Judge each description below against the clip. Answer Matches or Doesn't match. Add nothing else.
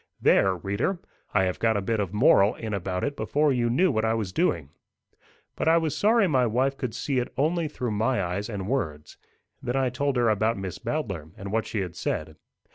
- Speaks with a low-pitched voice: Matches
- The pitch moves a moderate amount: Doesn't match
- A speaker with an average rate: Doesn't match